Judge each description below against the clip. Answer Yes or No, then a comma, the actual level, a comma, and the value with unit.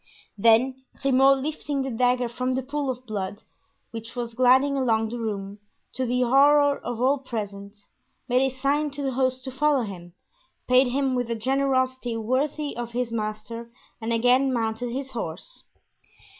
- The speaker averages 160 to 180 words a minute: Yes, average, 165 wpm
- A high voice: Yes, very high, 250 Hz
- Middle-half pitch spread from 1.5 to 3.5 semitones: Yes, average, 2.7 semitones